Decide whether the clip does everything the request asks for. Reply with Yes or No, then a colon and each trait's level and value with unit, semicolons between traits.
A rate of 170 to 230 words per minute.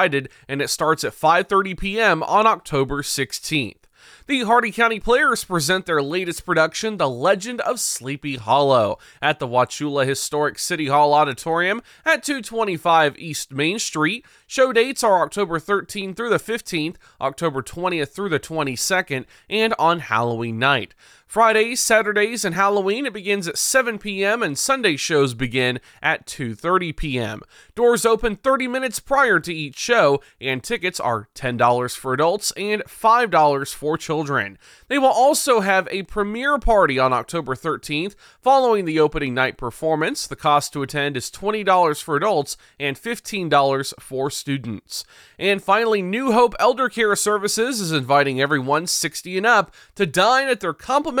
No: average, 155 wpm